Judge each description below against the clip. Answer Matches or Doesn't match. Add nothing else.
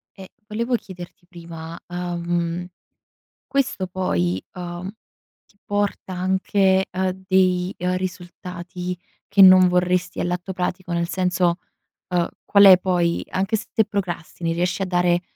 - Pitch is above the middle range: Doesn't match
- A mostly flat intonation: Matches